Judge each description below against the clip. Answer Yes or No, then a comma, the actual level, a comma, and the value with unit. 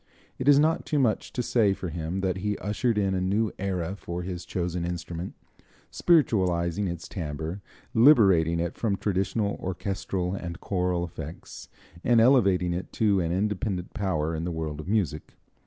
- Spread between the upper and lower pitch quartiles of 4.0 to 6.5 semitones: No, average, 3.2 semitones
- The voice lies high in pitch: No, very low, 95 Hz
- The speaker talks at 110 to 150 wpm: No, average, 165 wpm